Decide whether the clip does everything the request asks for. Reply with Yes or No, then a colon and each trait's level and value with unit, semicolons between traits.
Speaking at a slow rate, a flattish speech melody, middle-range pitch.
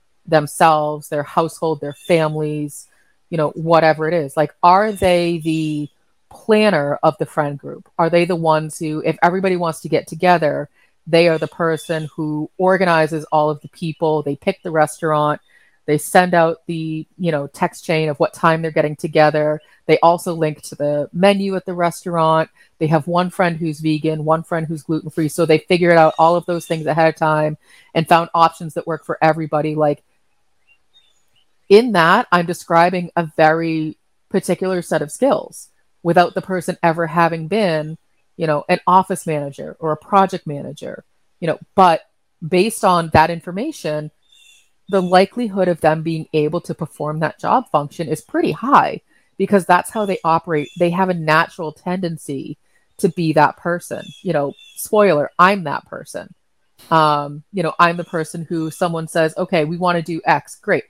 No: average, 175 wpm; narrow, 2.3 semitones; medium, 165 Hz